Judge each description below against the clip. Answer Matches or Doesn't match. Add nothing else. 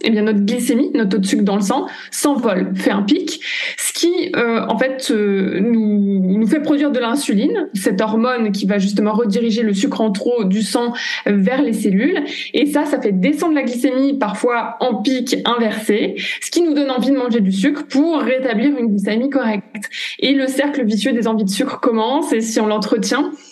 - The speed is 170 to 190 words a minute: Doesn't match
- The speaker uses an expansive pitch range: Doesn't match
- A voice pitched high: Matches